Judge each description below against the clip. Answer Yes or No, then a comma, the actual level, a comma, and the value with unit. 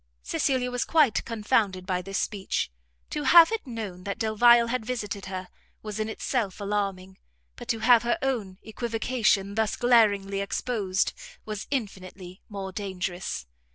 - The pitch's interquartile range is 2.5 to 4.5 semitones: Yes, average, 3.6 semitones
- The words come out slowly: No, average, 145 wpm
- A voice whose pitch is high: Yes, high, 210 Hz